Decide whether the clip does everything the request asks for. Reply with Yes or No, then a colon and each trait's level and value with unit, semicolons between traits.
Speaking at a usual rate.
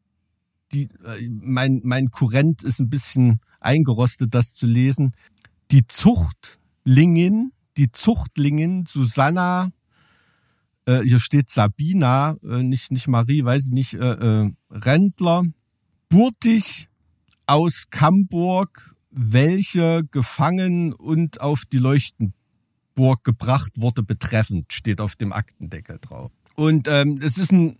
No: slow, 110 wpm